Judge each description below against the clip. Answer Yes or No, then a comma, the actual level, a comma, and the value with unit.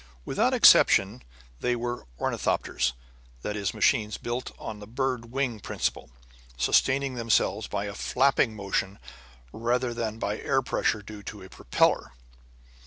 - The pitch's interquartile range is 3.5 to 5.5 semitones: No, average, 3.1 semitones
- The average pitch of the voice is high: No, low, 110 Hz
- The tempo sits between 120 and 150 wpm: Yes, slow, 135 wpm